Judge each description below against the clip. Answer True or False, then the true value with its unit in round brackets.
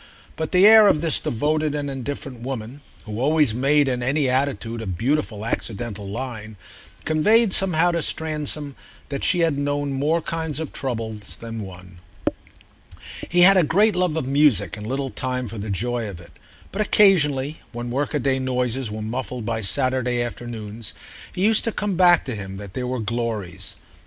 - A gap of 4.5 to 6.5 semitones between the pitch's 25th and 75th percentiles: True (5.2 semitones)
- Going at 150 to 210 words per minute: True (170 wpm)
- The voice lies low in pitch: True (130 Hz)